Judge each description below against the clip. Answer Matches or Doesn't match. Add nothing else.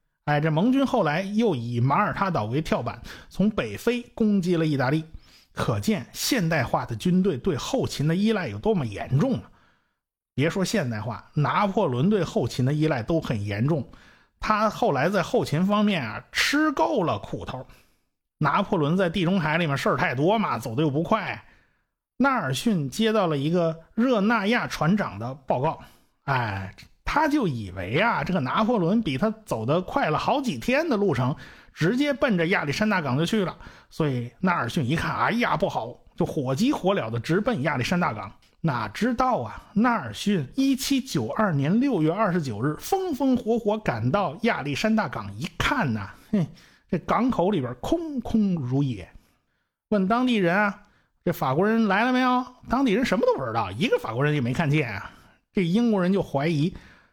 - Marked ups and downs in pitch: Matches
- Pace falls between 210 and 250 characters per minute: Doesn't match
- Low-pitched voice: Doesn't match